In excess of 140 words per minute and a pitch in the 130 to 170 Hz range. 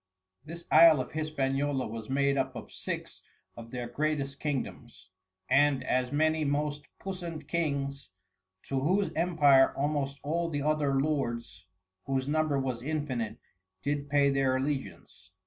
No: slow, 135 wpm; medium, 140 Hz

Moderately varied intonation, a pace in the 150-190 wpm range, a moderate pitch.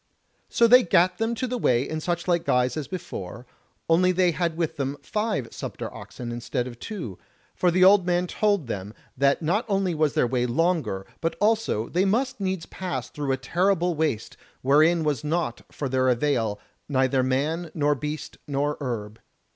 No: wide, 5.9 semitones; average, 180 wpm; medium, 155 Hz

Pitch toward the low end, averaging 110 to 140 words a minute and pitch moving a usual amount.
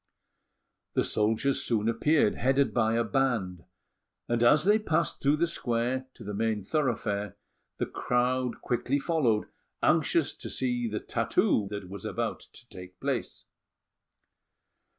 Yes: low, 120 Hz; slow, 135 wpm; average, 4.1 semitones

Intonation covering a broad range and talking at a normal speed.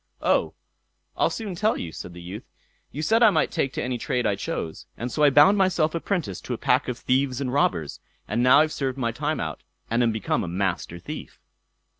No: wide, 7.5 semitones; fast, 220 wpm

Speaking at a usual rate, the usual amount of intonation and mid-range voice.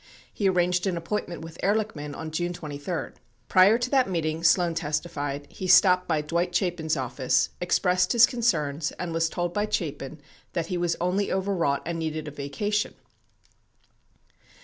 Yes: average, 155 wpm; average, 3.0 semitones; medium, 175 Hz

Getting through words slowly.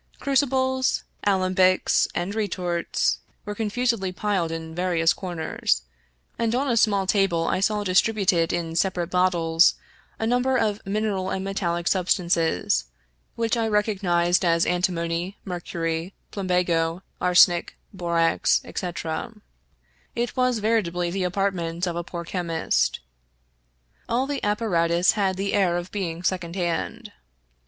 Yes: slow, 125 wpm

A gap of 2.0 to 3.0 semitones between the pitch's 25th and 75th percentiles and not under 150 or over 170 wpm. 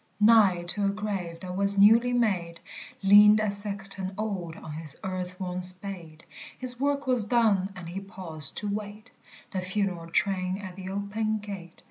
Yes: narrow, 2.5 semitones; average, 165 wpm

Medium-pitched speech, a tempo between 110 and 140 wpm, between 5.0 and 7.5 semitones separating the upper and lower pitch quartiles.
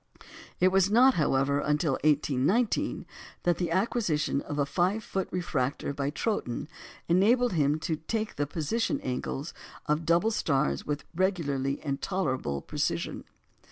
Yes: medium, 160 Hz; slow, 135 wpm; average, 5.3 semitones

